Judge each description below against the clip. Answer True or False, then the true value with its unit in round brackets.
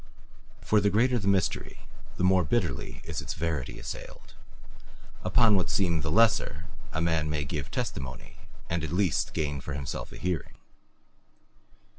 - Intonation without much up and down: False (4.6 semitones)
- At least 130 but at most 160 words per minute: True (150 wpm)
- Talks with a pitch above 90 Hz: False (85 Hz)